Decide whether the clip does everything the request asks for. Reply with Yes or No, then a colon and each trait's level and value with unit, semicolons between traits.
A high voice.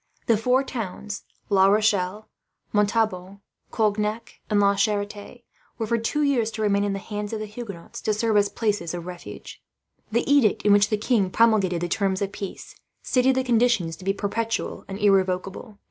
Yes: high, 210 Hz